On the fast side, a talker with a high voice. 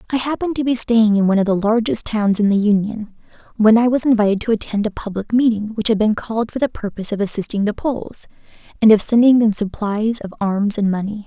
Yes: fast, 230 wpm; high, 215 Hz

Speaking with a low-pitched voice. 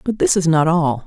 No: medium, 175 Hz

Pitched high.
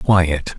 No: very low, 85 Hz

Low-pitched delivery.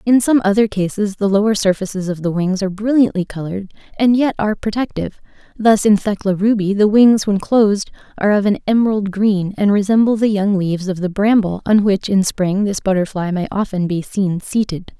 No: high, 200 Hz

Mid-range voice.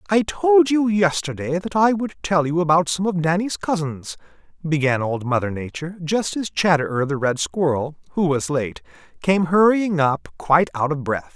Yes: medium, 165 Hz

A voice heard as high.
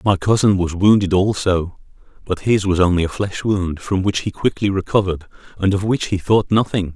No: very low, 95 Hz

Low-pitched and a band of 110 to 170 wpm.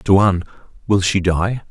Yes: very low, 95 Hz; average, 140 wpm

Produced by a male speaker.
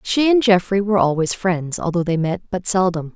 No: female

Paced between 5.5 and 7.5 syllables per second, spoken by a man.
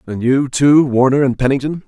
No: 5.2 syllables/s; male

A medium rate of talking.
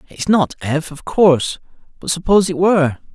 Yes: average, 170 wpm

